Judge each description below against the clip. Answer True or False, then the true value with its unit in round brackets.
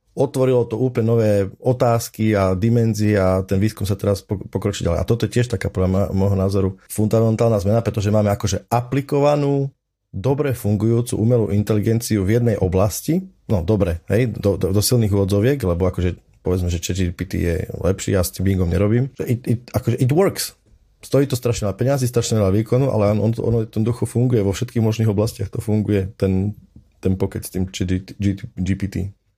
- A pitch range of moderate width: True (3.3 semitones)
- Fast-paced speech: True (180 wpm)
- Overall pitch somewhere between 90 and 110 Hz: True (105 Hz)